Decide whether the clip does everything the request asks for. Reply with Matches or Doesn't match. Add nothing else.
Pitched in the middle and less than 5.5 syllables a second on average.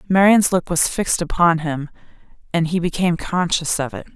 Matches